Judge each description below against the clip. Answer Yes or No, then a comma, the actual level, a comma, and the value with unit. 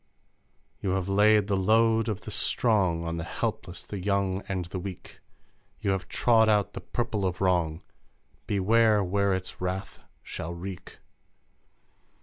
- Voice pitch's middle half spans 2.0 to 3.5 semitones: Yes, narrow, 2.4 semitones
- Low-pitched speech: Yes, very low, 95 Hz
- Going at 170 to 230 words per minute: No, average, 140 wpm